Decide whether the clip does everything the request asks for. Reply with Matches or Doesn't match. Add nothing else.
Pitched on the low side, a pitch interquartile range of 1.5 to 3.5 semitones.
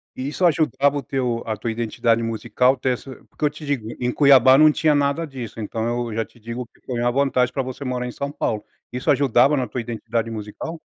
Matches